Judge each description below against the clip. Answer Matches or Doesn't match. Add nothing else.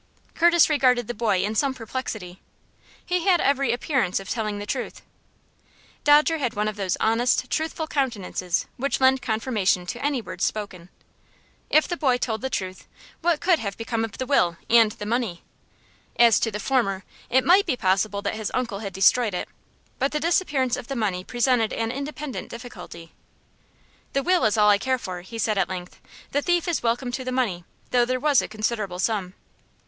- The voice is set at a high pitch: Matches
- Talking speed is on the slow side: Doesn't match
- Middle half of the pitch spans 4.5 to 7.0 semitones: Matches